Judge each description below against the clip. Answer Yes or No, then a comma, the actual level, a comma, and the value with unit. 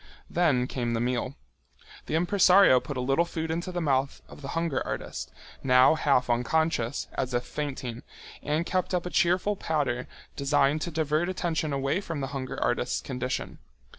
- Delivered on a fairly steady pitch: No, average, 4.5 semitones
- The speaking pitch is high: No, medium, 145 Hz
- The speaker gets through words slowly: No, average, 165 wpm